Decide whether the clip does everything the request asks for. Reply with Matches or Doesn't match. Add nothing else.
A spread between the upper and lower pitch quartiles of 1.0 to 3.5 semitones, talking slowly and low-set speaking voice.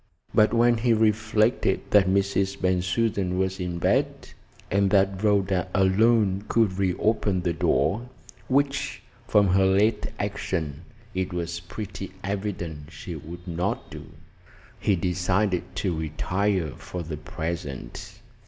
Matches